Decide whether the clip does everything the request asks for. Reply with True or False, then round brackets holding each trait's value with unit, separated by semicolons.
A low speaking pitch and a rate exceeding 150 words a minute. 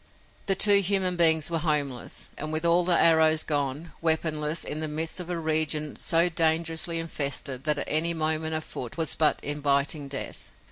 False (160 Hz; 170 wpm)